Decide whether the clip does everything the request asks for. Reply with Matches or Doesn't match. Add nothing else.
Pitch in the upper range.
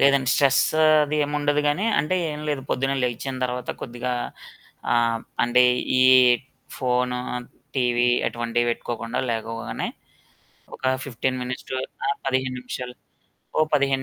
Doesn't match